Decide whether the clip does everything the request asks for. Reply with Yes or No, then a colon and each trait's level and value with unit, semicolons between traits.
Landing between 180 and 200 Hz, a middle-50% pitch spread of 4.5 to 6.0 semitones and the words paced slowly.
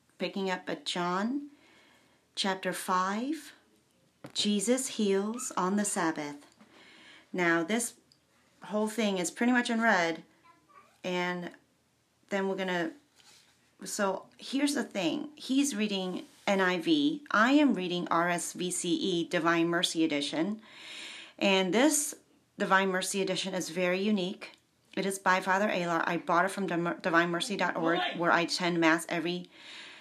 Yes: high, 190 Hz; average, 4.9 semitones; slow, 125 wpm